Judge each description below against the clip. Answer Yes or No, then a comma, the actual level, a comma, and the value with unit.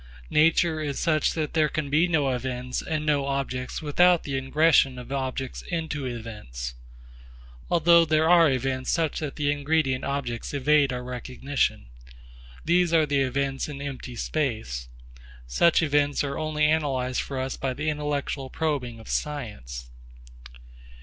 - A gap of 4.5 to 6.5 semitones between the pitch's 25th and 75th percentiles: No, average, 3.3 semitones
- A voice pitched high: No, medium, 140 Hz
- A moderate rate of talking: Yes, average, 145 wpm